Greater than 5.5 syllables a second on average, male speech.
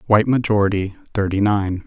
Yes: 5.9 syllables/s; male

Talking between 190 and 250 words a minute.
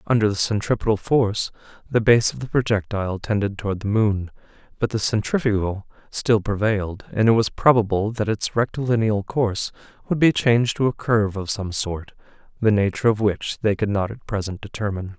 No: average, 180 wpm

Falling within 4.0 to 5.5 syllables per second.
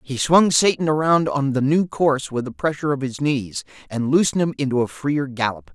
Yes: 5.4 syllables/s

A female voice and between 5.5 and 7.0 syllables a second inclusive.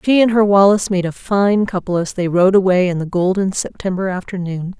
Yes: female; 5.6 syllables/s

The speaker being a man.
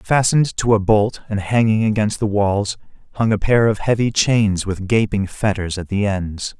Yes: male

